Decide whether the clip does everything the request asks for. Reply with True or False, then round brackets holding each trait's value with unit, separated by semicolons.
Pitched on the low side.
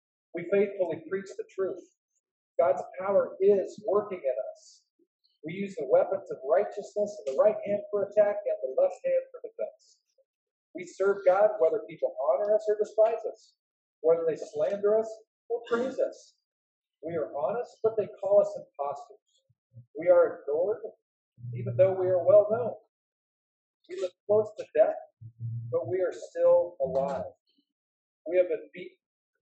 False (220 Hz)